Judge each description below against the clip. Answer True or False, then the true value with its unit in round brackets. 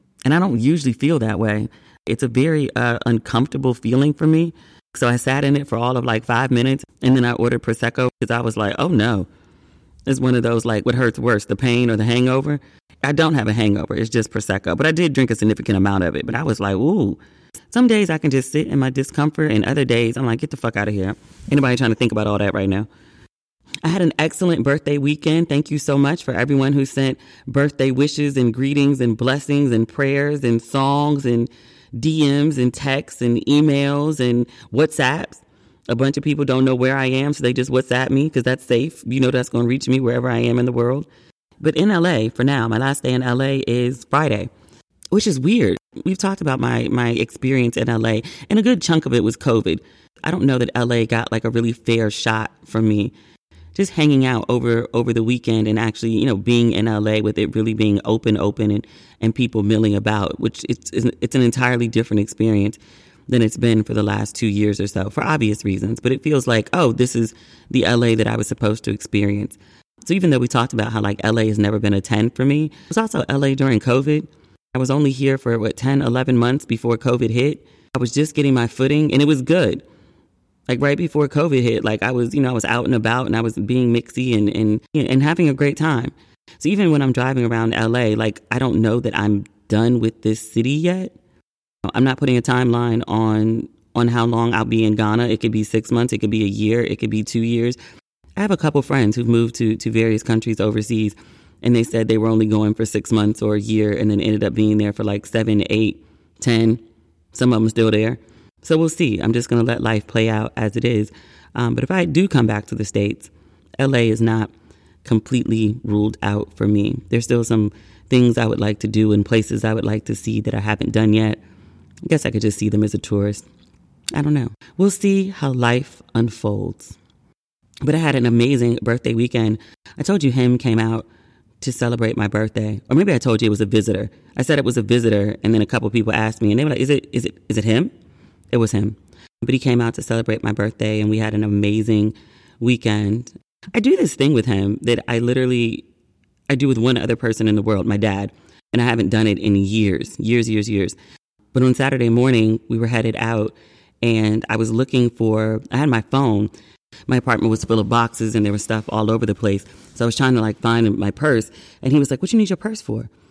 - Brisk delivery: True (235 wpm)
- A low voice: True (115 Hz)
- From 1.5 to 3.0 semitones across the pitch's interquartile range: False (3.4 semitones)